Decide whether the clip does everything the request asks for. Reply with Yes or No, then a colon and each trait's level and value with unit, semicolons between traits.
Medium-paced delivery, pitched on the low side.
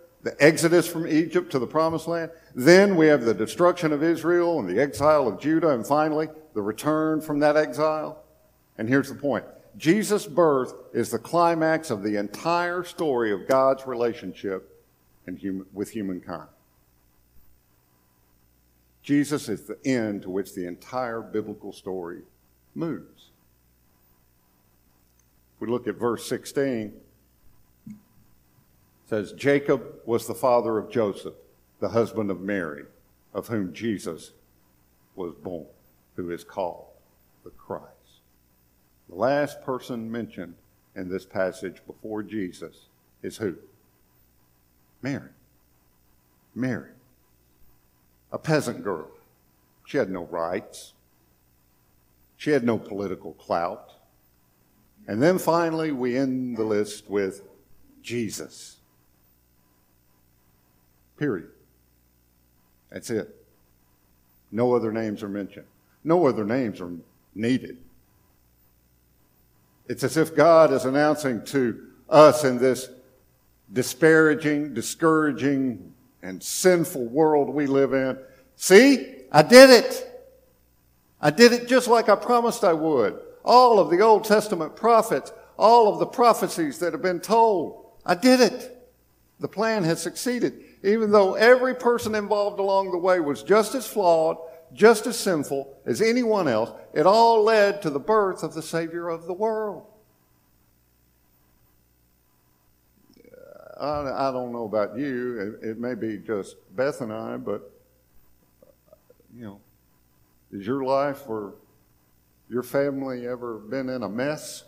No: slow, 125 wpm; low, 120 Hz